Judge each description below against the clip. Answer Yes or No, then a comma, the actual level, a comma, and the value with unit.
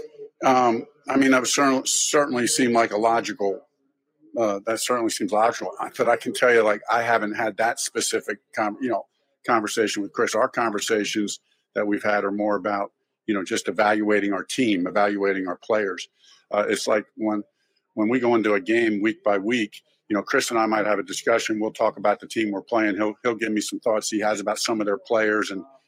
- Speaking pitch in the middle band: No, low, 110 Hz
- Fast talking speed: Yes, fast, 215 wpm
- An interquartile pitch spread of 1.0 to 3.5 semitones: Yes, narrow, 2.6 semitones